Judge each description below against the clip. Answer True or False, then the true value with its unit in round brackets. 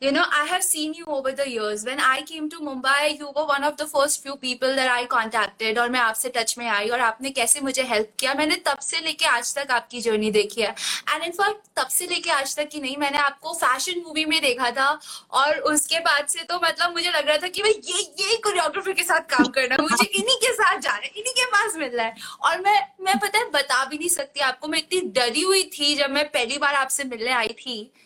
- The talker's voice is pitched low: False (290 Hz)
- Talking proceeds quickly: True (215 wpm)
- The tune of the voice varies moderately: True (4.6 semitones)